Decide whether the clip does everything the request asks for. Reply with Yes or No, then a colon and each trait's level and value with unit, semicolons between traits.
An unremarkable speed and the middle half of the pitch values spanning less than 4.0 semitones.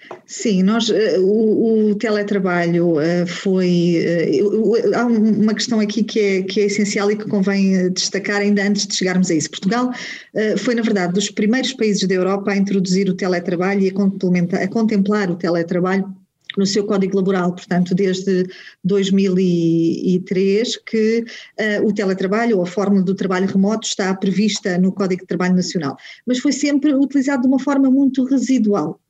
Yes: average, 160 wpm; narrow, 2.6 semitones